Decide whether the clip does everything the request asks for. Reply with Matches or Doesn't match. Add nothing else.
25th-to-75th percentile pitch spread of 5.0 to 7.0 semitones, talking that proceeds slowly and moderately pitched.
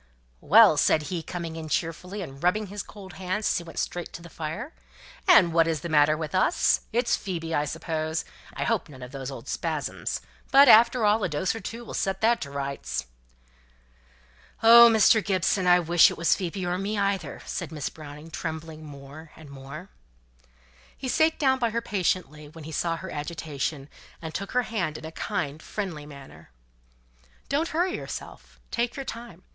Doesn't match